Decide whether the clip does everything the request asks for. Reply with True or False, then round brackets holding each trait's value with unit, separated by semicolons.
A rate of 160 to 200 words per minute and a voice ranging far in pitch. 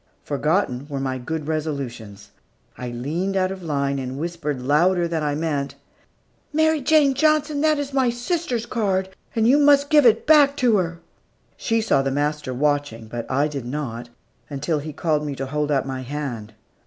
True (180 wpm; 8.9 semitones)